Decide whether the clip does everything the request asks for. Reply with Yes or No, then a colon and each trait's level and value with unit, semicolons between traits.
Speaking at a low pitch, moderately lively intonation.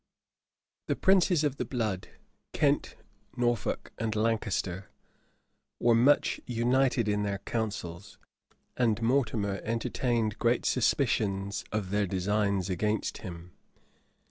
Yes: low, 110 Hz; average, 3.2 semitones